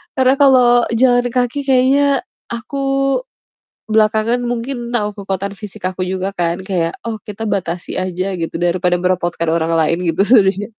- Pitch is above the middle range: Yes, high, 205 Hz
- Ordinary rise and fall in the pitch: Yes, average, 5.0 semitones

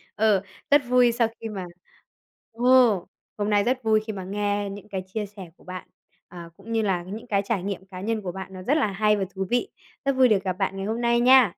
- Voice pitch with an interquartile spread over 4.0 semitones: No, average, 3.4 semitones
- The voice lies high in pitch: Yes, high, 205 Hz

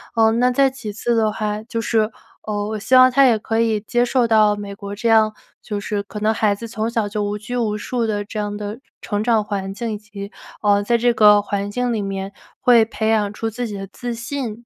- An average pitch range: No, narrow, 2.1 semitones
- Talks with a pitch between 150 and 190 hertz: No, high, 215 Hz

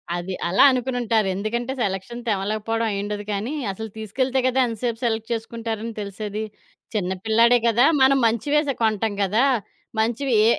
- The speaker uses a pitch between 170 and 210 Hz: No, high, 225 Hz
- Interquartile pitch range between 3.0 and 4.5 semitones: No, narrow, 2.6 semitones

